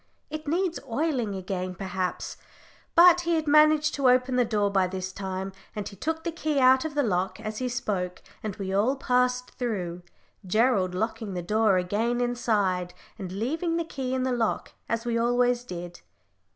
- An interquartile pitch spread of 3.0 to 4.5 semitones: No, wide, 5.6 semitones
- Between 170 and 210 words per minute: Yes, average, 180 wpm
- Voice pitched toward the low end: No, high, 230 Hz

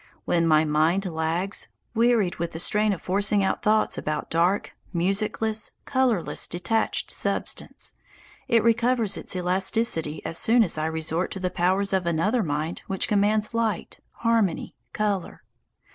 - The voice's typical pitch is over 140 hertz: Yes, high, 190 Hz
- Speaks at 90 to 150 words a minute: Yes, average, 145 wpm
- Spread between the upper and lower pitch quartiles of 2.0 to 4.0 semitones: No, average, 4.4 semitones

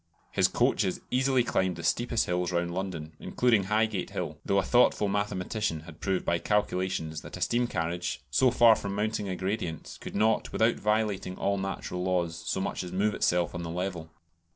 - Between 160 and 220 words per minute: Yes, average, 185 wpm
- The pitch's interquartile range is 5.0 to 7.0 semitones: No, average, 3.5 semitones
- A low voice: Yes, very low, 95 Hz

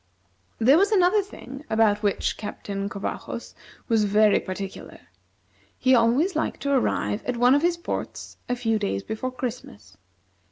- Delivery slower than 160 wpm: Yes, average, 150 wpm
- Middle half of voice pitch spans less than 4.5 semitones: No, average, 5.1 semitones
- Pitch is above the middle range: Yes, high, 235 Hz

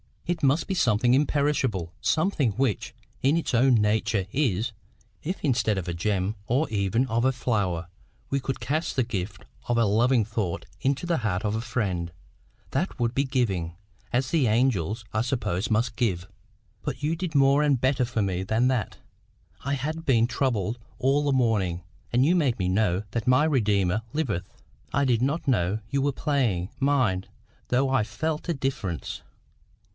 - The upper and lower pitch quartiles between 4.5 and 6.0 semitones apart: Yes, average, 4.9 semitones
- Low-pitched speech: Yes, low, 120 Hz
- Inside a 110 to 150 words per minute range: No, average, 170 wpm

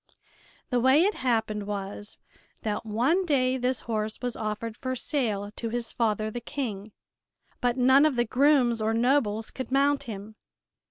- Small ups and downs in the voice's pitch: No, average, 3.4 semitones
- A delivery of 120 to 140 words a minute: No, average, 160 wpm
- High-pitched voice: Yes, high, 240 Hz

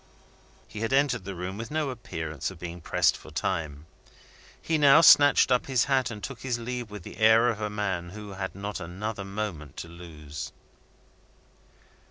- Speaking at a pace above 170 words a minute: Yes, average, 180 wpm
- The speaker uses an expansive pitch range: Yes, wide, 5.7 semitones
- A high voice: No, low, 105 Hz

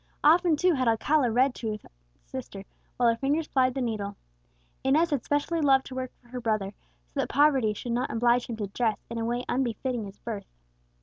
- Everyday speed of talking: No, fast, 210 wpm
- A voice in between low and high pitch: No, high, 245 Hz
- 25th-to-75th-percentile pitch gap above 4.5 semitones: No, average, 3.4 semitones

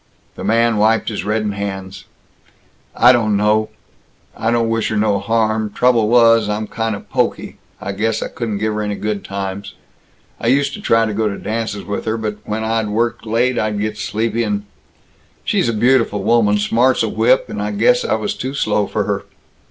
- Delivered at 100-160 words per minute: No, average, 200 wpm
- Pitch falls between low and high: No, low, 110 Hz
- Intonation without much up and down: Yes, narrow, 1.8 semitones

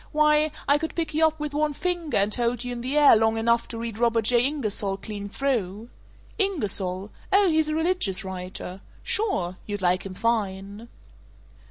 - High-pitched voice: Yes, high, 235 Hz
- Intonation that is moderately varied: No, wide, 7.1 semitones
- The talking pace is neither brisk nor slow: Yes, average, 180 wpm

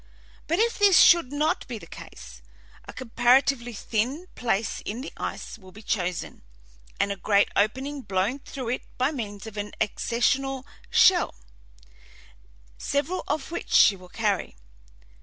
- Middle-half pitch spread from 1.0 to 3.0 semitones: No, average, 5.3 semitones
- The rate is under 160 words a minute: Yes, average, 145 wpm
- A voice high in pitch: Yes, high, 240 Hz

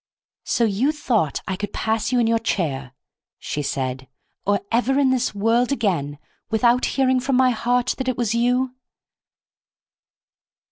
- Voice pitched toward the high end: Yes, high, 230 Hz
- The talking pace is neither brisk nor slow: Yes, average, 150 wpm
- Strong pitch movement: No, average, 4.2 semitones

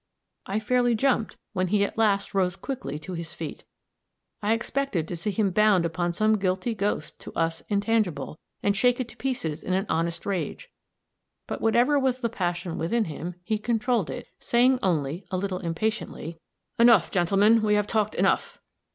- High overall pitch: Yes, high, 200 Hz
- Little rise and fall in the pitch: No, average, 4.6 semitones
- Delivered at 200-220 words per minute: No, average, 175 wpm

